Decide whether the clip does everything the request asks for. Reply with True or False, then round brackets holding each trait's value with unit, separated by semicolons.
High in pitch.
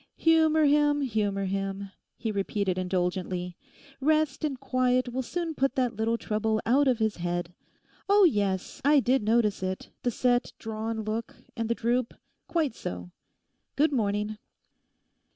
True (230 Hz)